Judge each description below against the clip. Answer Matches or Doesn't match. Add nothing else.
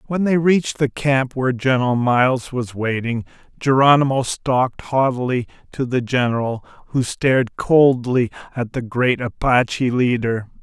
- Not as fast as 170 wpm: Matches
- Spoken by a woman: Doesn't match